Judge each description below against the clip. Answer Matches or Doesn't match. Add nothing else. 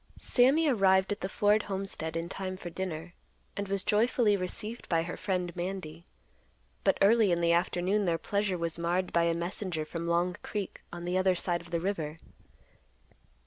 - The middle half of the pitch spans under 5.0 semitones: Matches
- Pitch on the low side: Doesn't match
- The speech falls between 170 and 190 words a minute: Matches